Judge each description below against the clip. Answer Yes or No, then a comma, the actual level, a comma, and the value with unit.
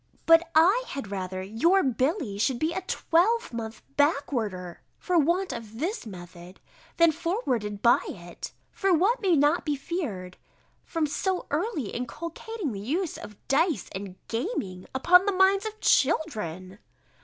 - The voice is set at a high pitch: Yes, very high, 290 Hz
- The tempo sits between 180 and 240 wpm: No, average, 145 wpm